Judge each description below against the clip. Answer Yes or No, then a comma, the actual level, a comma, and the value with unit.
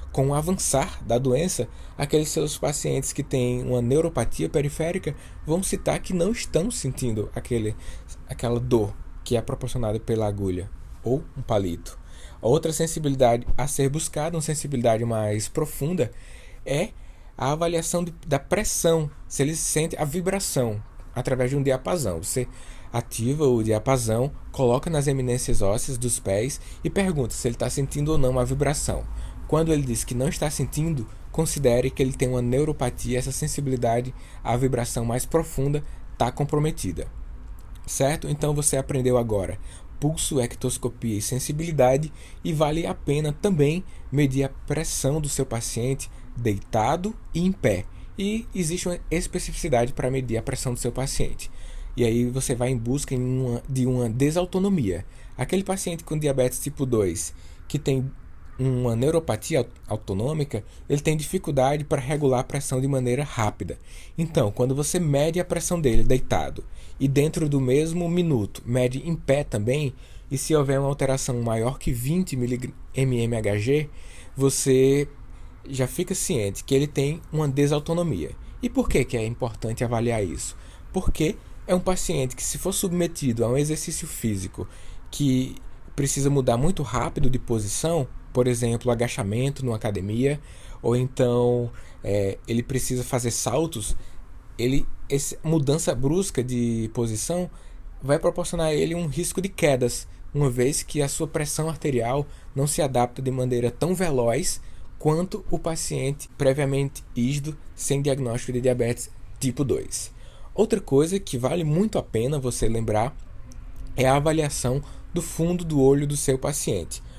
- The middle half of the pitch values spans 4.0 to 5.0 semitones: Yes, average, 4.3 semitones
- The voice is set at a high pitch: No, low, 135 Hz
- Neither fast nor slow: Yes, average, 150 wpm